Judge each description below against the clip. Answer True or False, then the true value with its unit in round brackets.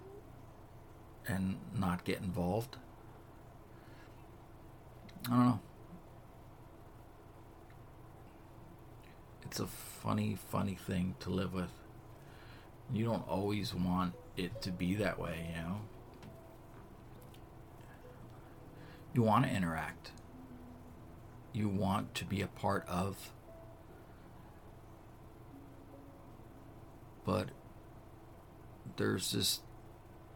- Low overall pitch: True (110 Hz)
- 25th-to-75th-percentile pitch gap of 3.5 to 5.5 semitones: False (2.9 semitones)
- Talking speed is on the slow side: True (80 wpm)